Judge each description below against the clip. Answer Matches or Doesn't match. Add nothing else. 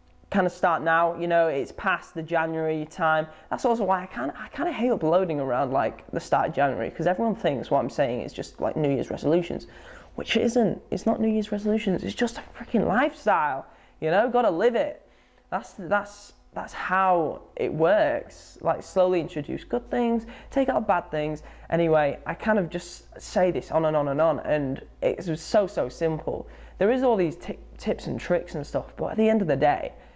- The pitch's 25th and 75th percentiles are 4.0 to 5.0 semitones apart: Doesn't match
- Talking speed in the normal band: Doesn't match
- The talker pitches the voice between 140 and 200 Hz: Matches